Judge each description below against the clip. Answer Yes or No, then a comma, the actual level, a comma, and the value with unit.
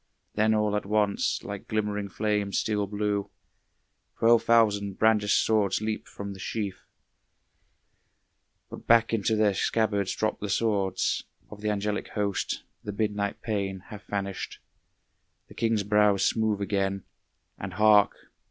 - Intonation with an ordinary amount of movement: No, narrow, 1.3 semitones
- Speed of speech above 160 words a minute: No, slow, 135 wpm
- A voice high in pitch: No, low, 105 Hz